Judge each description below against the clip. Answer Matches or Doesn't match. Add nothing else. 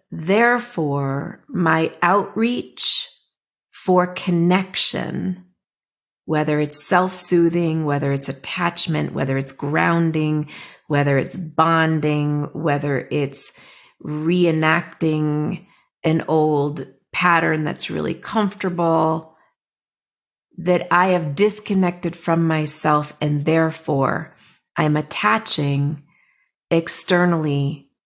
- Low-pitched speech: Doesn't match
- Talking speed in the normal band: Doesn't match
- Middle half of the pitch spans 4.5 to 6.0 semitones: Doesn't match